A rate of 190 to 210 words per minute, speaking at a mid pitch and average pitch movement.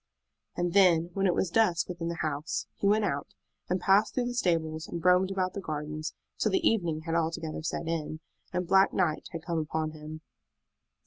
Yes: average, 195 wpm; medium, 170 Hz; average, 3.2 semitones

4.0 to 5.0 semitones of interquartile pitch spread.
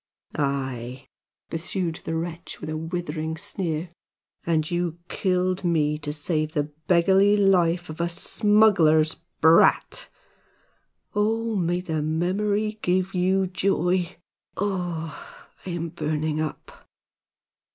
No: average, 3.0 semitones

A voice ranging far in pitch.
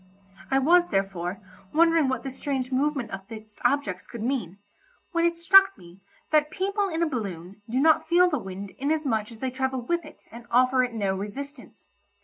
Yes: wide, 6.9 semitones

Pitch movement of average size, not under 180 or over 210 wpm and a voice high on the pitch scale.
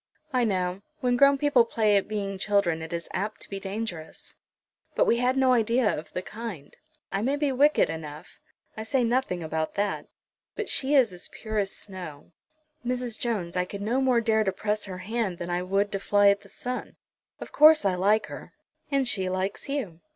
Yes: average, 4.9 semitones; average, 200 wpm; high, 210 Hz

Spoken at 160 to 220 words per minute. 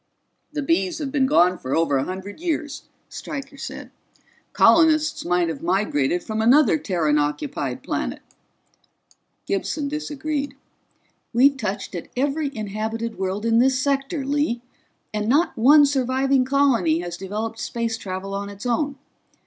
No: average, 140 wpm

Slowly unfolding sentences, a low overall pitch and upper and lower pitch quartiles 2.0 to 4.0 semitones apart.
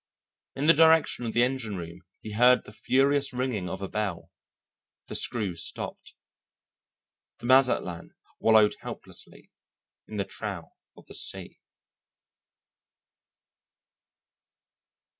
No: slow, 110 wpm; low, 110 Hz; average, 4.8 semitones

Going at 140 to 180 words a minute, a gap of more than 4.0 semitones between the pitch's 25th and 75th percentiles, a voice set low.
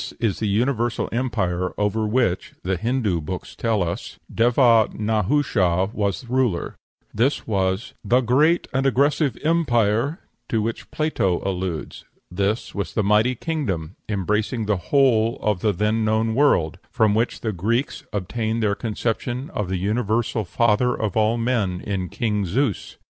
No: average, 150 wpm; average, 3.5 semitones; low, 110 Hz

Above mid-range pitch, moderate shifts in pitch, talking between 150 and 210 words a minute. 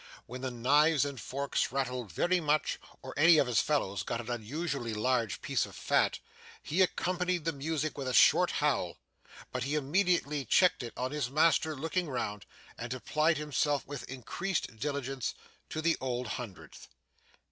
No: medium, 140 Hz; average, 4.1 semitones; average, 165 wpm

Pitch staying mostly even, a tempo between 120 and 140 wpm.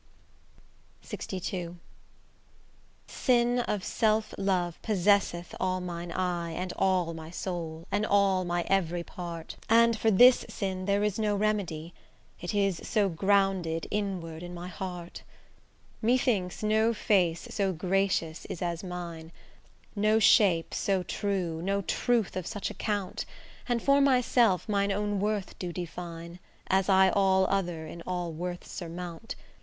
No: average, 3.0 semitones; slow, 135 wpm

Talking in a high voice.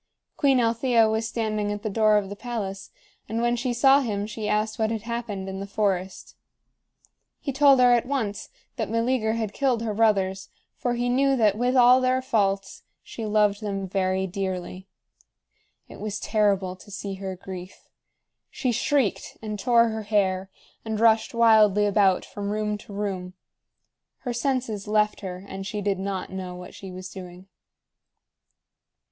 Yes: high, 210 Hz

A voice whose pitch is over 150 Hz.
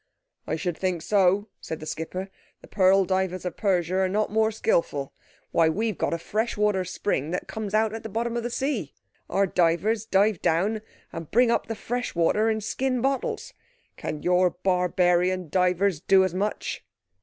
Yes: high, 190 Hz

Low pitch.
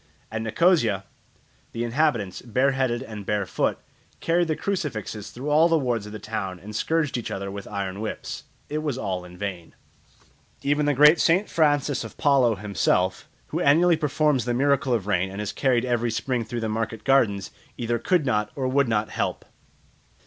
Yes: low, 120 Hz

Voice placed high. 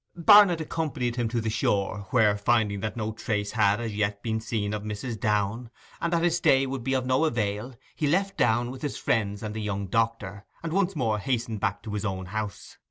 No: low, 110 Hz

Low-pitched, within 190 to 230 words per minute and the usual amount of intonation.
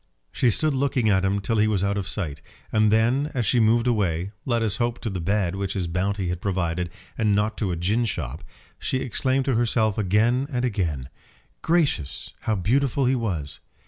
Yes: low, 105 Hz; average, 200 wpm; average, 4.5 semitones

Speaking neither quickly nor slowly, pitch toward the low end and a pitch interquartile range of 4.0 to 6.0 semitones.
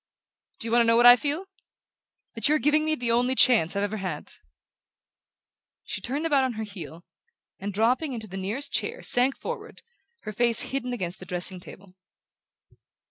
No: average, 180 wpm; high, 235 Hz; average, 5.1 semitones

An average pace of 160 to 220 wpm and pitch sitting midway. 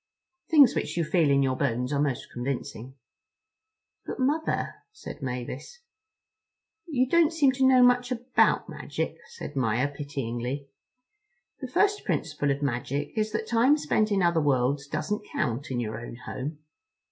No: average, 150 wpm; medium, 150 Hz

